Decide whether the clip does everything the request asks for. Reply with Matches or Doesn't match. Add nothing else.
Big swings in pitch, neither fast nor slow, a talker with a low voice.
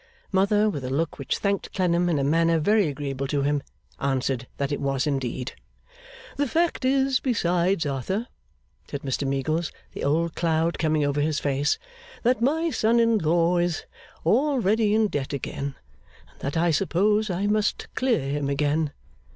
Doesn't match